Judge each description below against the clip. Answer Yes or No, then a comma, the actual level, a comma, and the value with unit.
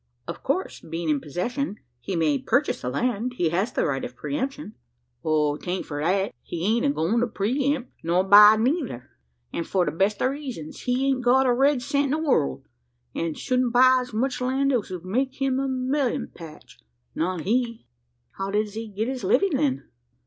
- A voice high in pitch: Yes, high, 230 Hz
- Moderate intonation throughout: No, wide, 7.0 semitones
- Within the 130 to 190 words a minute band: No, average, 200 wpm